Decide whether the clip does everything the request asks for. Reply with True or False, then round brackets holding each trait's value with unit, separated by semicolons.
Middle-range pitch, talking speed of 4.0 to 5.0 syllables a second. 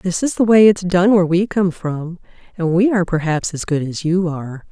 False (180 Hz; 5.4 syllables/s)